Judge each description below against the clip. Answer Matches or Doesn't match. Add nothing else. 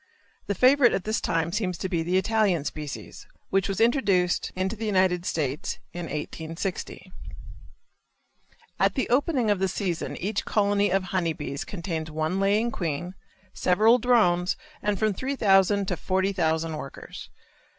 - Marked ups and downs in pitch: Doesn't match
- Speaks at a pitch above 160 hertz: Matches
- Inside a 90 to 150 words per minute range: Matches